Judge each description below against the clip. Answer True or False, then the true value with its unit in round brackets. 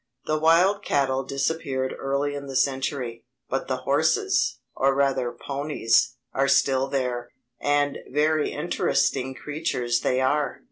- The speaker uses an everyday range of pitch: False (1.9 semitones)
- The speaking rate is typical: False (130 wpm)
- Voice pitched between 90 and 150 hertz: True (135 Hz)